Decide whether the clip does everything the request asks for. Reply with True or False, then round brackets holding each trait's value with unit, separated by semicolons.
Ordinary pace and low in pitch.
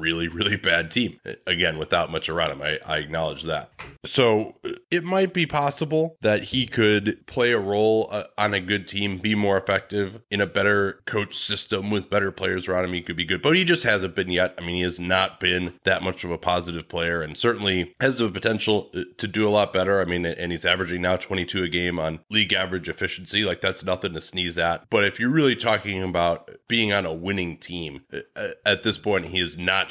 False (220 wpm; 95 Hz)